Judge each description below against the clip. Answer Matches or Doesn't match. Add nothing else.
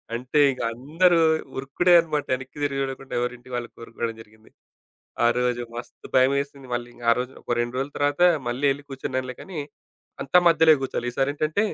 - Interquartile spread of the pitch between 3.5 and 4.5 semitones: Doesn't match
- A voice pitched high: Doesn't match